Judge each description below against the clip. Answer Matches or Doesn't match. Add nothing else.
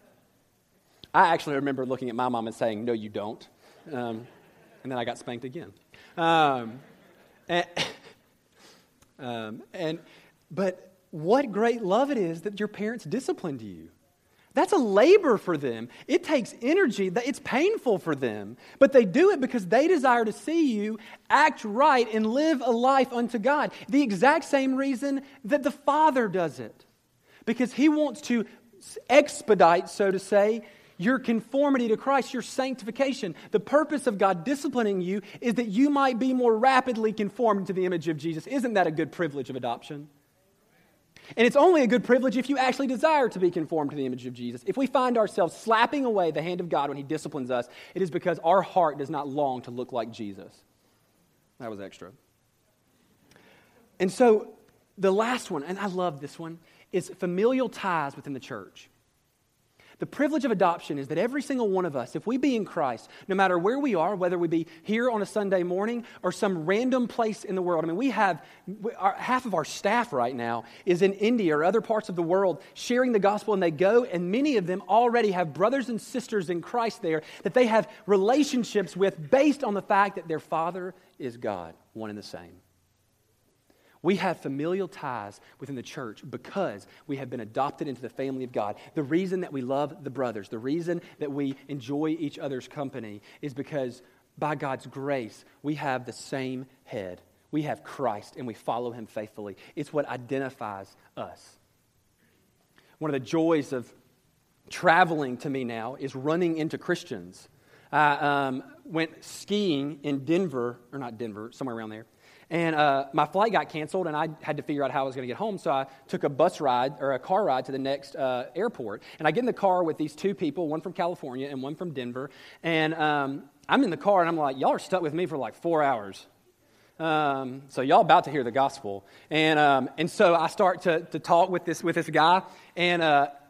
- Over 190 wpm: Matches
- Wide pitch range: Matches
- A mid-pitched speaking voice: Matches